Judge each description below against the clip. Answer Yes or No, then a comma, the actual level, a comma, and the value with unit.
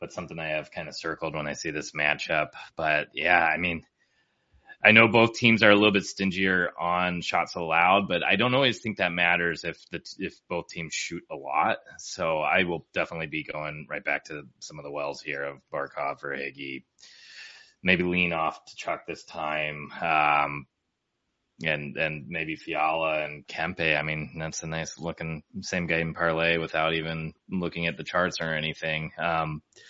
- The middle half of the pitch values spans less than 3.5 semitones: Yes, average, 2.7 semitones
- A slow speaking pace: No, average, 185 wpm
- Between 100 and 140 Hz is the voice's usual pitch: No, very low, 80 Hz